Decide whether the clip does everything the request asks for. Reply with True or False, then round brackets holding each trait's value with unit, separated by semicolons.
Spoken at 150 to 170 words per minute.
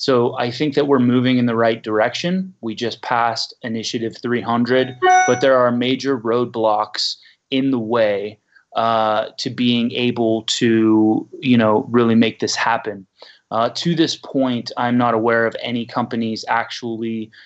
True (155 wpm)